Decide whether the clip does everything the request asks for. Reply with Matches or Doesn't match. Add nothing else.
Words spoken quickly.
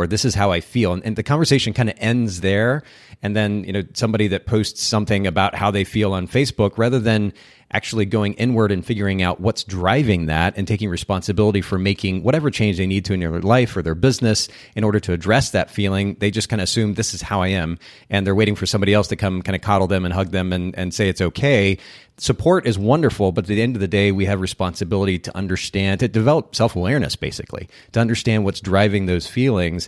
Matches